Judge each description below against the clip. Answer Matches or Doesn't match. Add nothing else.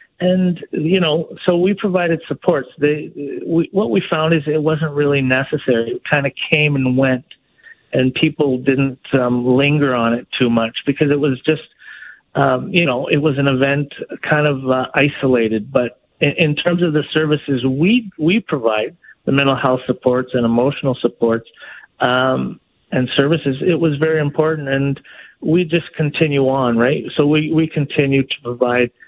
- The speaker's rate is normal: Matches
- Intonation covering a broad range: Doesn't match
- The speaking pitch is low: Doesn't match